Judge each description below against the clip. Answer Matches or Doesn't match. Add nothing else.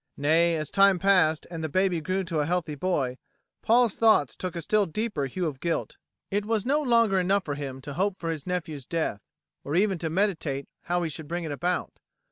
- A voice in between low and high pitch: Matches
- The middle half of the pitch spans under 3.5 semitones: Doesn't match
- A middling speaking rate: Doesn't match